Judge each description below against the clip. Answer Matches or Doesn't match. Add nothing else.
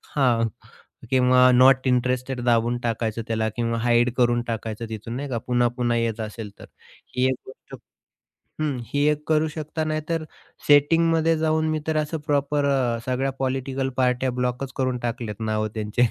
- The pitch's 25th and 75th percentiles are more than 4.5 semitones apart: Doesn't match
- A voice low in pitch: Matches